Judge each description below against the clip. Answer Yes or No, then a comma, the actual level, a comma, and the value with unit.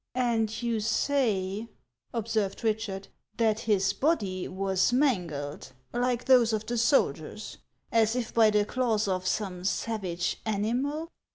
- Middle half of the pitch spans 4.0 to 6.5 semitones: No, average, 3.5 semitones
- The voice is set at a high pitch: Yes, high, 220 Hz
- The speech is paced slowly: Yes, slow, 130 wpm